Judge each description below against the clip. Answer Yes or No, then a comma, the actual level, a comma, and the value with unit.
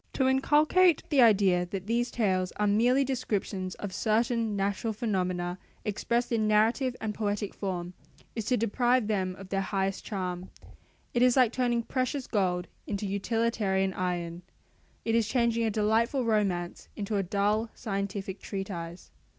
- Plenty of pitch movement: No, average, 3.5 semitones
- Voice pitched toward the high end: Yes, high, 210 Hz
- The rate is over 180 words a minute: No, average, 150 wpm